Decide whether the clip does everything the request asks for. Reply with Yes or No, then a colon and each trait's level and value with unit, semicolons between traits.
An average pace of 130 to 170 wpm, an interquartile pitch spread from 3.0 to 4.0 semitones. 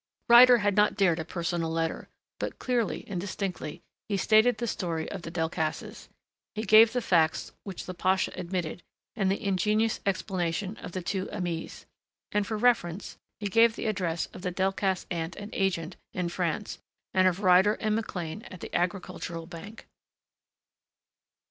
Yes: average, 160 wpm; average, 3.3 semitones